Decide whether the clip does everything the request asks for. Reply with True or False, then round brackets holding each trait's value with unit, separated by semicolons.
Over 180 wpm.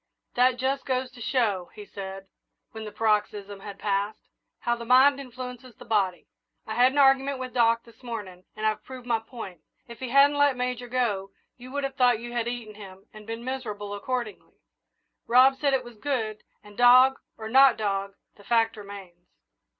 True (190 wpm)